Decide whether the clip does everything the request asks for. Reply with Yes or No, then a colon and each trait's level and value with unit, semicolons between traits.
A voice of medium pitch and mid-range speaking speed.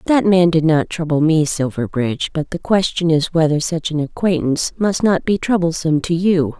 Yes: medium, 165 Hz; average, 190 wpm